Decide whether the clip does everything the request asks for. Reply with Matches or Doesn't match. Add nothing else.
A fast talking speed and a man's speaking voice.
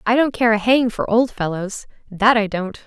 Doesn't match